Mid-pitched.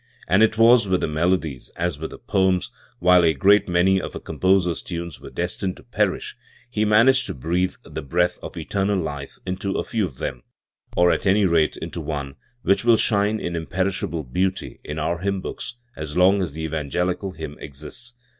No: very low, 90 Hz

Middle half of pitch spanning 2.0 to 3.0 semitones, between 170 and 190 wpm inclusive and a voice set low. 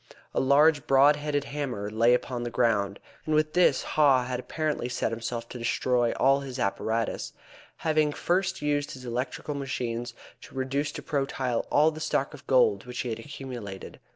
No: average, 3.6 semitones; average, 175 wpm; low, 130 Hz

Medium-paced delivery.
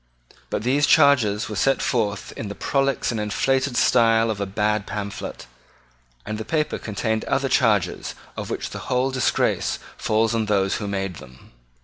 Yes: average, 165 wpm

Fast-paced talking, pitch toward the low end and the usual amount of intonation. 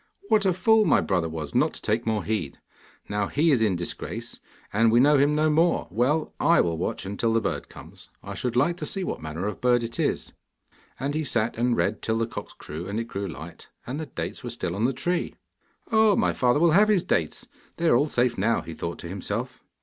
No: fast, 235 wpm; low, 120 Hz; wide, 7.2 semitones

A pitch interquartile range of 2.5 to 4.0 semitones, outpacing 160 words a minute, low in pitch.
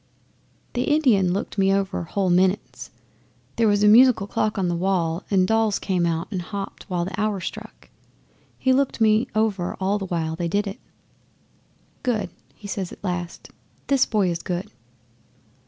No: average, 3.3 semitones; average, 170 wpm; high, 195 Hz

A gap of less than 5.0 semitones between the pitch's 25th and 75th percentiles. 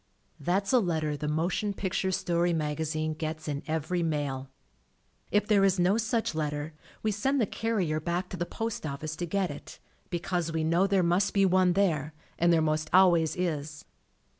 Yes: average, 3.6 semitones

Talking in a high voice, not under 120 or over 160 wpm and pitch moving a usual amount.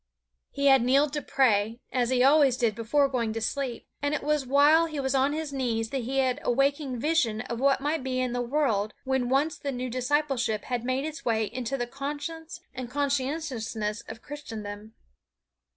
No: very high, 260 Hz; average, 195 wpm; average, 3.2 semitones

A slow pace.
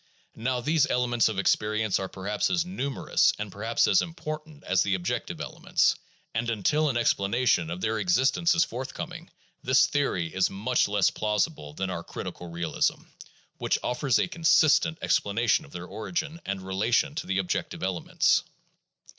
No: average, 160 wpm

